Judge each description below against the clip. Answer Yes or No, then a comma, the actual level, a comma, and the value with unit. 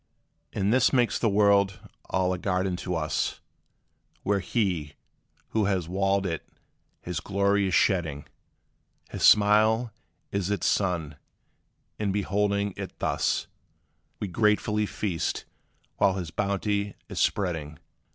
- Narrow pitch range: Yes, narrow, 2.3 semitones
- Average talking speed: No, slow, 120 wpm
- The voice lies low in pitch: Yes, low, 100 Hz